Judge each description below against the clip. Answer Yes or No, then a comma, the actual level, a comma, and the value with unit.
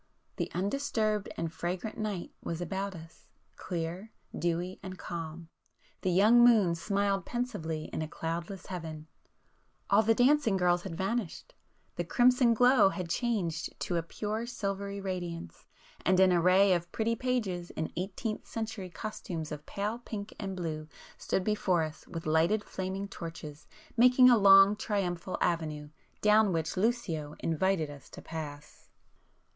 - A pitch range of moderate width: Yes, average, 4.3 semitones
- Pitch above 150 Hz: Yes, high, 190 Hz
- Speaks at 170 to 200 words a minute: No, average, 140 wpm